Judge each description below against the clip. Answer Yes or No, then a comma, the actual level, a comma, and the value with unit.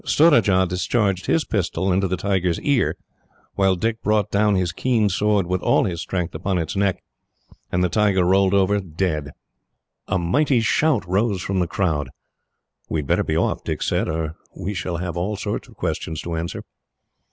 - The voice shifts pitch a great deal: No, average, 2.9 semitones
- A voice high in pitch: No, very low, 95 Hz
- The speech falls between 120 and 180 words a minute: Yes, average, 175 wpm